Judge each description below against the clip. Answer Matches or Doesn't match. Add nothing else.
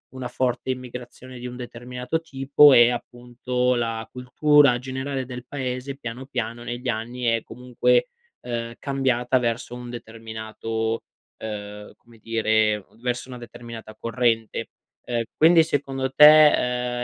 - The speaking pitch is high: Doesn't match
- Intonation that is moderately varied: Doesn't match